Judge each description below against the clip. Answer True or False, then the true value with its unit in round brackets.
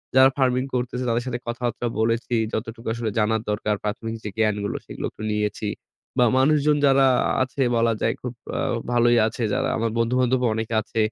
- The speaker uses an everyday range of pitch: False (2.3 semitones)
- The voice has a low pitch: True (120 Hz)